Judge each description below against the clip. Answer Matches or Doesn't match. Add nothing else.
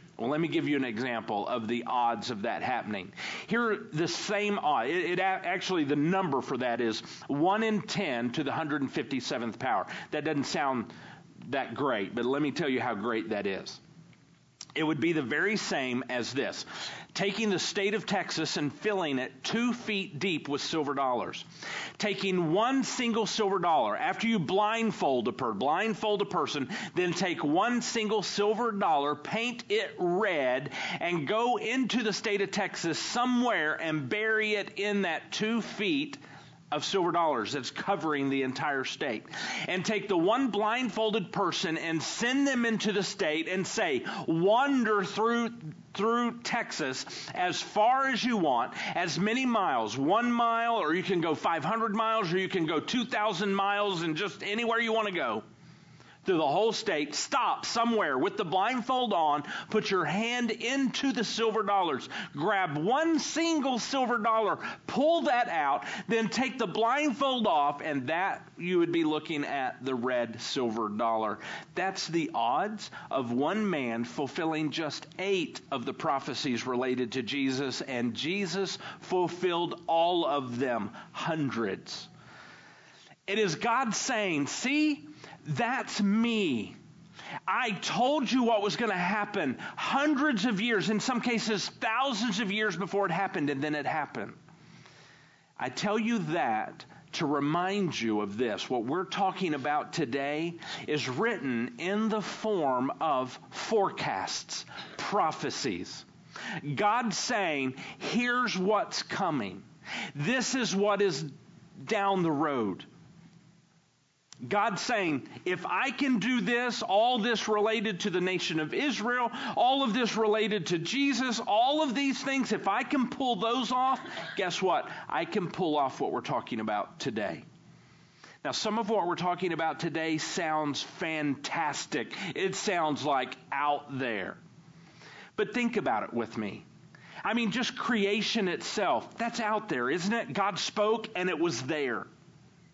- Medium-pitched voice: Doesn't match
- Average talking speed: Matches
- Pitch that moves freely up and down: Matches